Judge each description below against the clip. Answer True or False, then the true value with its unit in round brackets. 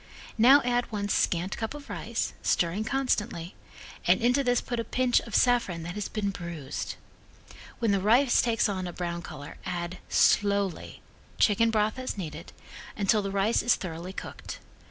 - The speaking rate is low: False (165 wpm)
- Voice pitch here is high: True (205 Hz)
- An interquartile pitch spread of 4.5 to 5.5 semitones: True (5.0 semitones)